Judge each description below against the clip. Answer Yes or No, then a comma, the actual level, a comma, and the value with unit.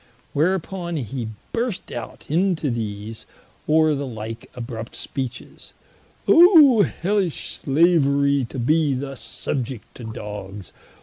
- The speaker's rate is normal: No, slow, 110 wpm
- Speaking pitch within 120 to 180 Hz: Yes, medium, 140 Hz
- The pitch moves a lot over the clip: Yes, wide, 6.7 semitones